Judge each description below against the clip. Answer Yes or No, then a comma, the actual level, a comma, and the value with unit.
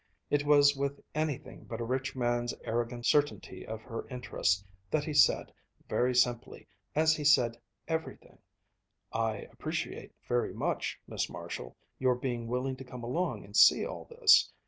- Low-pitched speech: Yes, low, 125 Hz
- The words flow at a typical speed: Yes, average, 155 wpm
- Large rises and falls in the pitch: No, average, 3.4 semitones